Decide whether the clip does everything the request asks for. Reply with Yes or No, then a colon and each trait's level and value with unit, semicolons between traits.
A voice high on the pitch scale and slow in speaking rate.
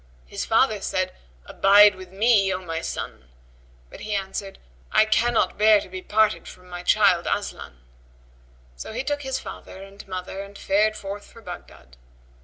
No: high, 195 Hz; average, 165 wpm